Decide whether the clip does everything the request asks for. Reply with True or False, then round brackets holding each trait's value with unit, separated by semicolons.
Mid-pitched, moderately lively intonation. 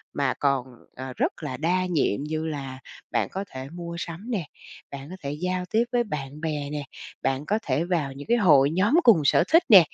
True (155 Hz; 4.9 semitones)